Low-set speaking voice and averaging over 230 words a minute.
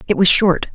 No: medium, 185 Hz; fast, 240 wpm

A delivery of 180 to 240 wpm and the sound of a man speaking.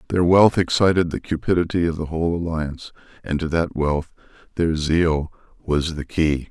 No: average, 165 wpm; male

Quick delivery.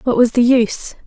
Yes: fast, 225 wpm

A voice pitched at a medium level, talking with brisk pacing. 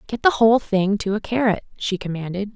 No: high, 205 Hz; fast, 210 wpm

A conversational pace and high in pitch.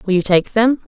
No: fast, 255 wpm; high, 210 Hz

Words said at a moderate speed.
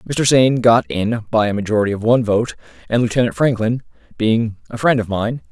Yes: average, 195 wpm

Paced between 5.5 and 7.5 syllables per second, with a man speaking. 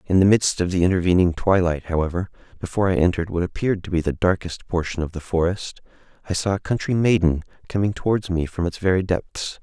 Yes: 6.3 syllables/s; male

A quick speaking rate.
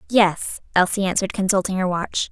No: average, 155 wpm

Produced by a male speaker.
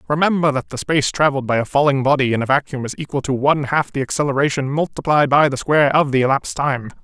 Yes: male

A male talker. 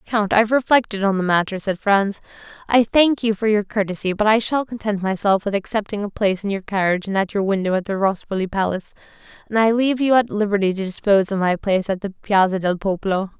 No: female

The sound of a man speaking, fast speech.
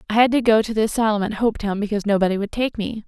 No: female; fast, 275 wpm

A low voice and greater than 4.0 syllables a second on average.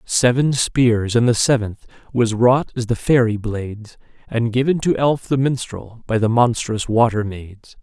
Yes: low, 120 Hz; 4.3 syllables/s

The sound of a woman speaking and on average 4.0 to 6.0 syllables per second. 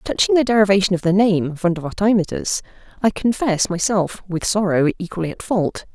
Yes: female; 5.5 syllables/s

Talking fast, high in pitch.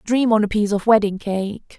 Yes: fast, 235 wpm; high, 210 Hz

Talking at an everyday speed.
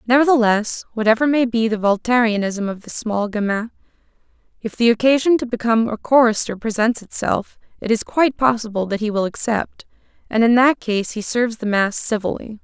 Yes: average, 170 wpm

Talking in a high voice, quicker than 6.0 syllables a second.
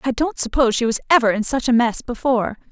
Yes: high, 245 Hz; 6.6 syllables/s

